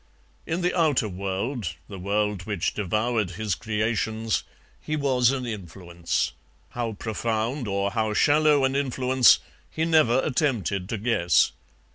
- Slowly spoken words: Yes, slow, 130 wpm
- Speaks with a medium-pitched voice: No, low, 110 Hz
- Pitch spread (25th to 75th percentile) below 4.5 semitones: No, average, 4.8 semitones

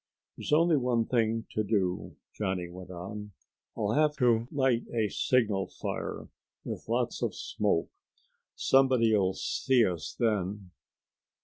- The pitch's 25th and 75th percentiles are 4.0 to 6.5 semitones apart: Yes, average, 4.4 semitones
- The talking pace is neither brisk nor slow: No, slow, 125 wpm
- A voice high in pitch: No, low, 110 Hz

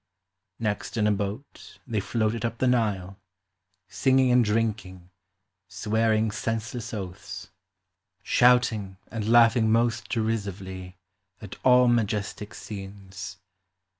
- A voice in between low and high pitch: No, low, 110 Hz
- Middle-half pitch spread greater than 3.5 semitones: No, average, 2.9 semitones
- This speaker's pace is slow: Yes, slow, 110 wpm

